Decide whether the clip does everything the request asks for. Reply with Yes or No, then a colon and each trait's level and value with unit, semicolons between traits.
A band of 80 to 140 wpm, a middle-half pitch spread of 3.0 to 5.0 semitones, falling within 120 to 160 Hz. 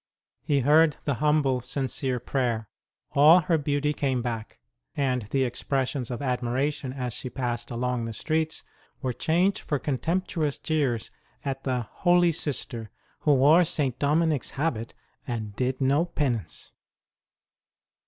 Yes: slow, 135 wpm; average, 3.4 semitones; low, 135 Hz